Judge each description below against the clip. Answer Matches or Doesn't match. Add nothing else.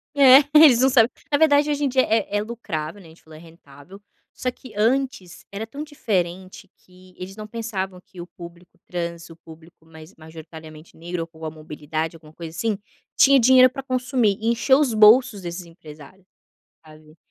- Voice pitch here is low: Doesn't match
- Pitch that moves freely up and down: Matches